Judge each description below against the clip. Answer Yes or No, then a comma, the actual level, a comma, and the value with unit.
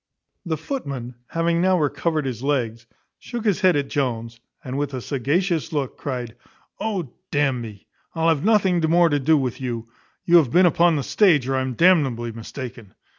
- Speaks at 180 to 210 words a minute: Yes, average, 185 wpm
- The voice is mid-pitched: Yes, medium, 145 Hz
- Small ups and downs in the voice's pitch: No, average, 5.3 semitones